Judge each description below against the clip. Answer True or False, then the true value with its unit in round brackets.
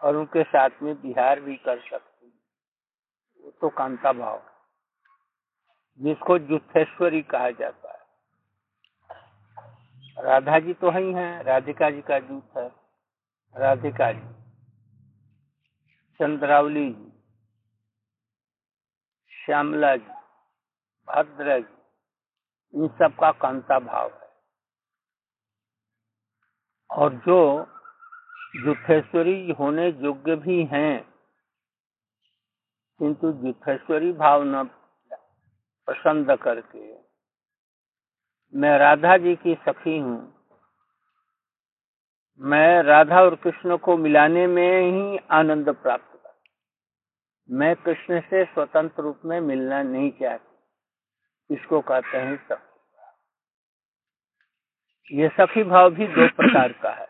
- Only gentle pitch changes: False (4.7 semitones)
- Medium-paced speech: False (95 wpm)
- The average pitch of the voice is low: False (150 Hz)